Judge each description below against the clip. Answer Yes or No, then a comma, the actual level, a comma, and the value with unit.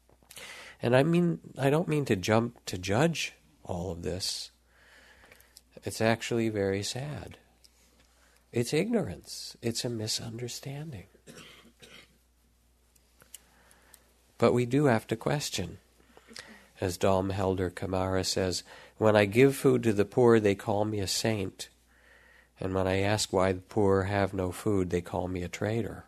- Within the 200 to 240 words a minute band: No, average, 140 wpm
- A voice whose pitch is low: Yes, very low, 95 Hz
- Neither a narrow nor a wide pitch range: Yes, average, 5.0 semitones